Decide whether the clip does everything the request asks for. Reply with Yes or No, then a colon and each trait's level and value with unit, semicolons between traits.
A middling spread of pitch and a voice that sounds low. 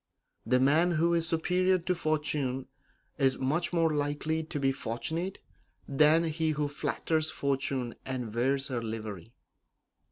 No: average, 3.7 semitones; medium, 145 Hz